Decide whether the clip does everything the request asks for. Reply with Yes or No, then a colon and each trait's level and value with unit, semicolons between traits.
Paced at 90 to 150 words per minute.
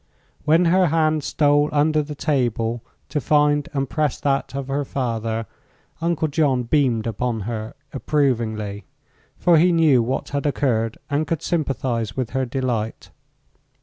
Yes: average, 145 wpm